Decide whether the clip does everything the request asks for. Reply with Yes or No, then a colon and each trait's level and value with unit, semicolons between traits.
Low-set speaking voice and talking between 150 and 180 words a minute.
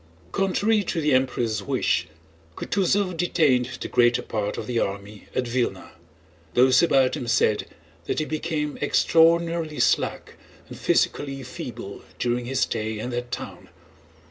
No: low, 130 Hz; average, 140 wpm